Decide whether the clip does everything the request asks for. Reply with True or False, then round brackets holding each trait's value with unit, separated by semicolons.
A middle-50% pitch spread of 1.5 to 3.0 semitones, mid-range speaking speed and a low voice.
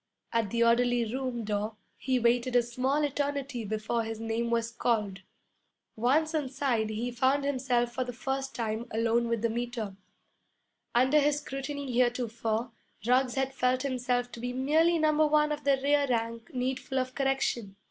False (2.7 semitones; 160 wpm; 245 Hz)